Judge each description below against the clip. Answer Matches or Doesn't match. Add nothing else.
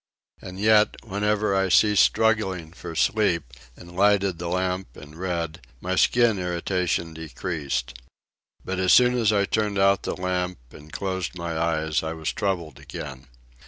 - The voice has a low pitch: Matches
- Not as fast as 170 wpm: Matches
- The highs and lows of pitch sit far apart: Doesn't match